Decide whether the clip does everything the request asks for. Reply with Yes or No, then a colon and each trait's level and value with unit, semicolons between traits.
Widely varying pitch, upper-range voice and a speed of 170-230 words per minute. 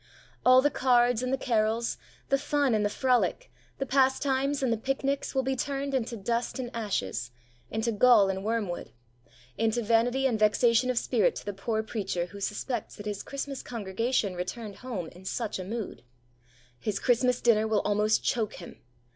No: average, 3.6 semitones; high, 230 Hz; average, 175 wpm